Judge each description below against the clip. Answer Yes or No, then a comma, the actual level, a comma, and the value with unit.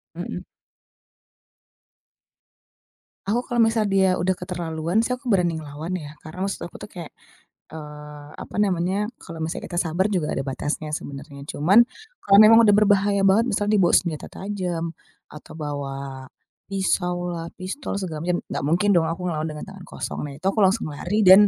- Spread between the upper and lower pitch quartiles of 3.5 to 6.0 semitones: Yes, average, 3.9 semitones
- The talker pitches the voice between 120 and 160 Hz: No, medium, 175 Hz